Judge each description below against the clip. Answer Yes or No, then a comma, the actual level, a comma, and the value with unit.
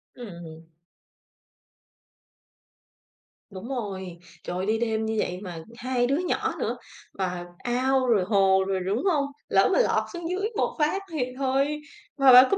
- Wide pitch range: Yes, wide, 6.2 semitones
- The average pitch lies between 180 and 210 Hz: No, high, 235 Hz